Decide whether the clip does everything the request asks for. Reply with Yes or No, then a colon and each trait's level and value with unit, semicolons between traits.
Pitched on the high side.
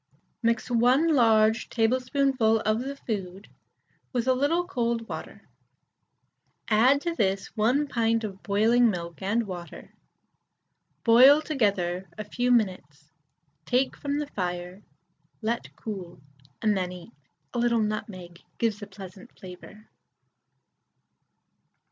Yes: high, 225 Hz